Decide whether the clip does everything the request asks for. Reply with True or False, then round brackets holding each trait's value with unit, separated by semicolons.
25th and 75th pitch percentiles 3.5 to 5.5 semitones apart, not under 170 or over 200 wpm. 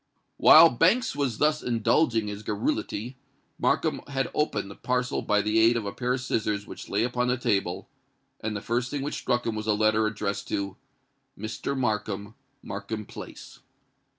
False (3.1 semitones; 175 wpm)